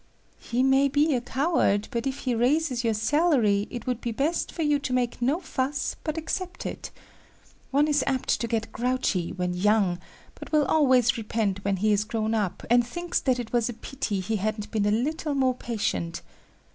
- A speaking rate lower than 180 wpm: No, average, 195 wpm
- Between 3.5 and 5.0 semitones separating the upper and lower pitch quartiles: Yes, average, 4.5 semitones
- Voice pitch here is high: Yes, high, 245 Hz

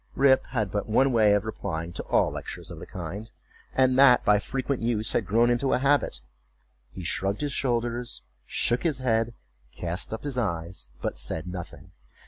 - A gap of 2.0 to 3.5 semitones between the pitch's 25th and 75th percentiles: No, wide, 5.5 semitones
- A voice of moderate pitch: No, low, 115 Hz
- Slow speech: No, average, 180 wpm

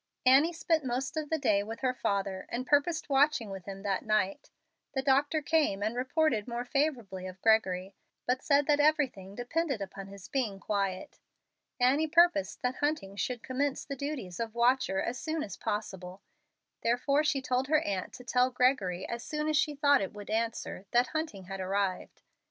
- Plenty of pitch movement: Yes, wide, 6.3 semitones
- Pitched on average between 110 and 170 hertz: No, high, 245 Hz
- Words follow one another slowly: No, average, 180 wpm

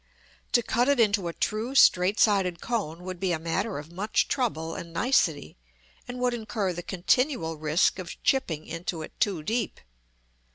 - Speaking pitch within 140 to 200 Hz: Yes, high, 190 Hz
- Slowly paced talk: No, average, 170 wpm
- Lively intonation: Yes, wide, 5.7 semitones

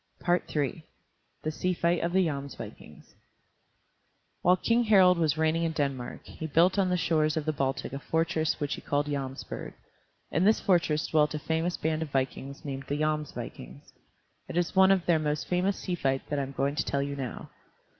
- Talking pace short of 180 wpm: No, average, 190 wpm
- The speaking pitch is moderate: Yes, medium, 155 Hz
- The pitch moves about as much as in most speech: Yes, average, 3.6 semitones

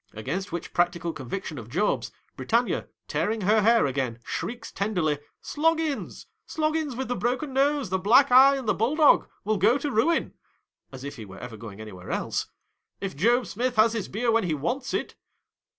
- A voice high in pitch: Yes, high, 215 Hz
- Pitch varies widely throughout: Yes, wide, 8.5 semitones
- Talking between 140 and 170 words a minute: No, average, 200 wpm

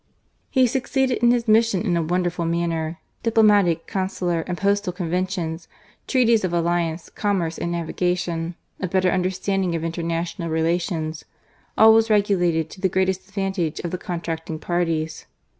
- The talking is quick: No, average, 155 wpm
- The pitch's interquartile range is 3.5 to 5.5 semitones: No, average, 3.0 semitones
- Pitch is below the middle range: No, medium, 180 Hz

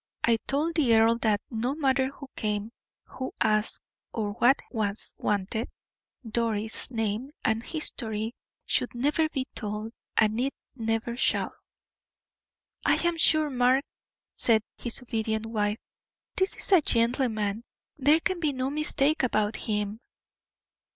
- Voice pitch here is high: Yes, high, 230 Hz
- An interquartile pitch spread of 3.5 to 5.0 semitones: Yes, average, 3.9 semitones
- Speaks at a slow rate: Yes, slow, 130 wpm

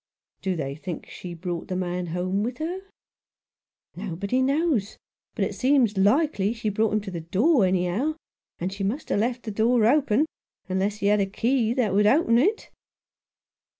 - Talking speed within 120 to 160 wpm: No, average, 185 wpm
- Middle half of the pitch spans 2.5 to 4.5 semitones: No, average, 5.2 semitones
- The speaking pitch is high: Yes, high, 210 Hz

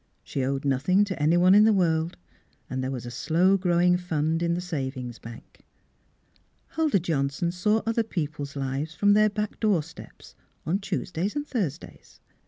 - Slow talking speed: No, average, 170 wpm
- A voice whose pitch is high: No, medium, 170 Hz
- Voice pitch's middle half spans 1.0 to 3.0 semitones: No, wide, 5.4 semitones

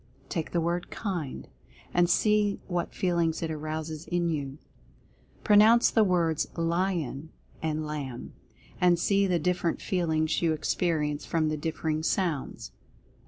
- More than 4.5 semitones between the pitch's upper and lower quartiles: No, narrow, 2.4 semitones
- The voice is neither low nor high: Yes, medium, 165 Hz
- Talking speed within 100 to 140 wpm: Yes, slow, 135 wpm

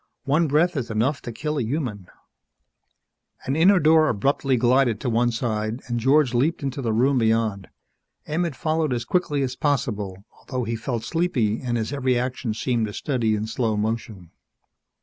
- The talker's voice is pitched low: Yes, low, 125 Hz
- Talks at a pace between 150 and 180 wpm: Yes, average, 175 wpm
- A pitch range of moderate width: Yes, average, 4.2 semitones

